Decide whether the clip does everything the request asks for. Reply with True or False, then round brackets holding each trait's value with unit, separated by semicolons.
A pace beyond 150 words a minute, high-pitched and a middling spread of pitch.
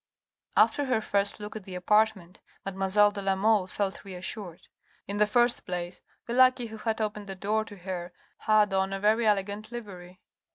False (180 wpm; 205 Hz; 2.3 semitones)